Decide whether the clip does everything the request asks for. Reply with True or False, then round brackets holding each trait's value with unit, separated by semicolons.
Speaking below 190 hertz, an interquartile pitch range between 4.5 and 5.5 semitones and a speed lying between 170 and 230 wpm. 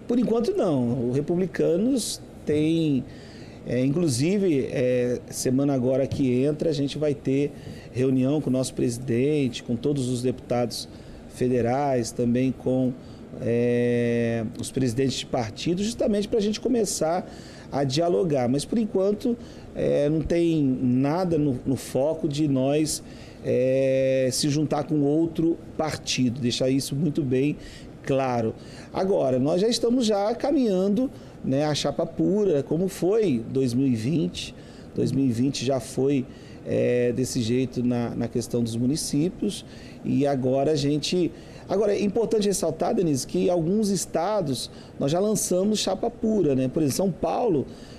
False (140 Hz; 5.2 semitones; 140 wpm)